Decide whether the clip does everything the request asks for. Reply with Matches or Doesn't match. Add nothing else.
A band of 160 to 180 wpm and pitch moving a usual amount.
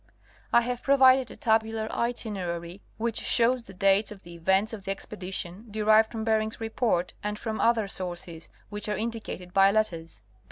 Matches